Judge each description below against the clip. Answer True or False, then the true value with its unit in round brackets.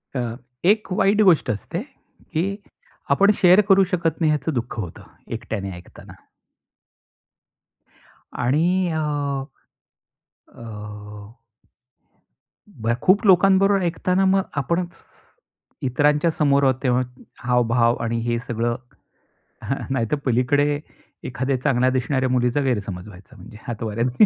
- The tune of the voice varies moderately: False (6.8 semitones)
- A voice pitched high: False (135 Hz)